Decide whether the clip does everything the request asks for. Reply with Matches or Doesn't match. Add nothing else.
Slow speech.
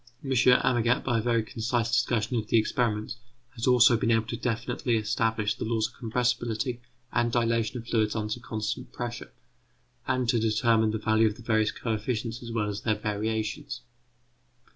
Doesn't match